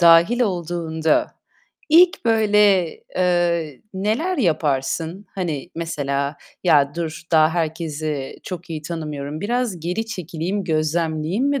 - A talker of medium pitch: Yes, medium, 170 Hz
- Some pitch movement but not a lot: Yes, average, 4.0 semitones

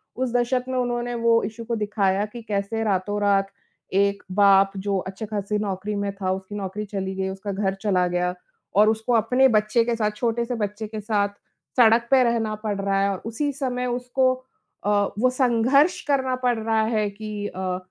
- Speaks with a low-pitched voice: No, high, 215 Hz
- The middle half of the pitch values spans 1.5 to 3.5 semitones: Yes, average, 3.1 semitones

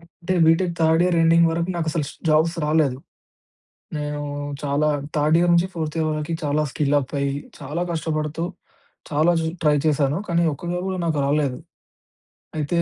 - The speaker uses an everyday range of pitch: No, narrow, 2.3 semitones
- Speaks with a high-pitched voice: No, medium, 155 Hz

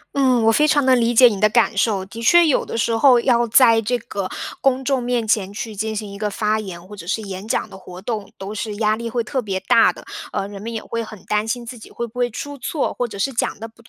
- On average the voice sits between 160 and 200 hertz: No, high, 225 Hz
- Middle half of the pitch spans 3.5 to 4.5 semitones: No, average, 2.9 semitones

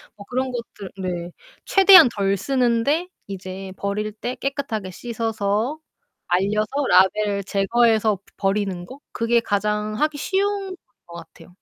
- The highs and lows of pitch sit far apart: No, average, 4.2 semitones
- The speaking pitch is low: No, high, 210 Hz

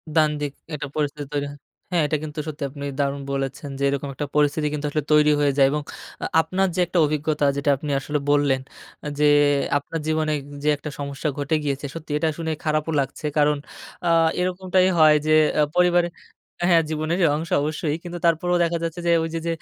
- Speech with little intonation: Yes, narrow, 2.2 semitones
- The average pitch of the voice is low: No, medium, 150 Hz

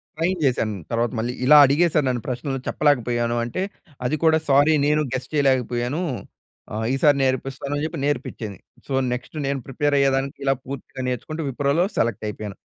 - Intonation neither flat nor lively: Yes, average, 3.2 semitones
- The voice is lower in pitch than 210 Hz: Yes, low, 135 Hz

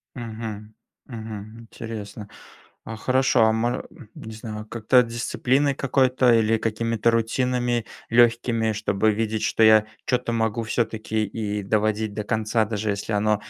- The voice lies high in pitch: No, low, 110 Hz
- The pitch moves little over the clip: Yes, narrow, 1.5 semitones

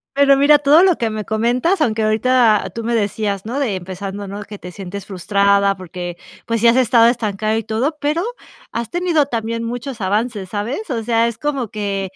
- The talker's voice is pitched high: Yes, high, 225 Hz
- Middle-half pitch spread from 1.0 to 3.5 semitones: No, average, 4.1 semitones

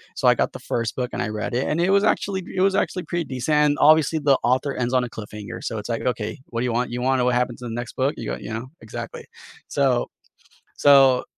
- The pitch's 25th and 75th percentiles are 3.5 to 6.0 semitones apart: Yes, average, 3.8 semitones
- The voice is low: Yes, low, 125 Hz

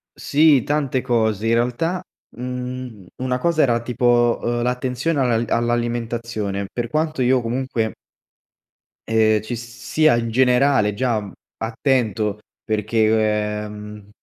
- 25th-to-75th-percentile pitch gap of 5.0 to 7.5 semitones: No, narrow, 2.6 semitones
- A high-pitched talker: No, low, 120 Hz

